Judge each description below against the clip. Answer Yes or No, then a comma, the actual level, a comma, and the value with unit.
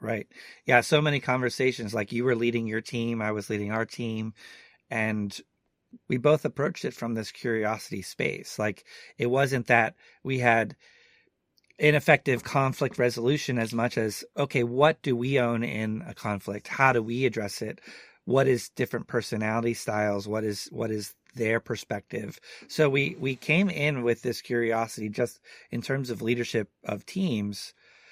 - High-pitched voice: No, low, 120 Hz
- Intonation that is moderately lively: Yes, average, 3.3 semitones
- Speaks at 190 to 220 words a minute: No, average, 160 wpm